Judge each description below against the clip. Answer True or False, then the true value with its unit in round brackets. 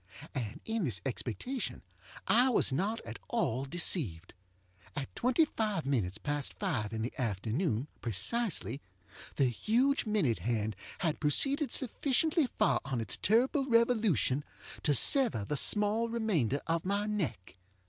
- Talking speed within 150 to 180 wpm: False (135 wpm)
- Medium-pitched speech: True (170 Hz)